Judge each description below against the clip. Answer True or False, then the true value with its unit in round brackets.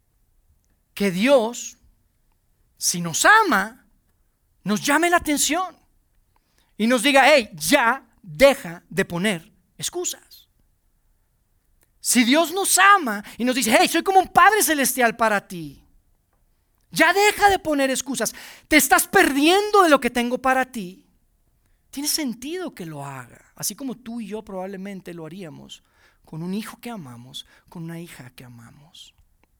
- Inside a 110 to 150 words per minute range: True (140 wpm)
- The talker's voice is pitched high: True (220 Hz)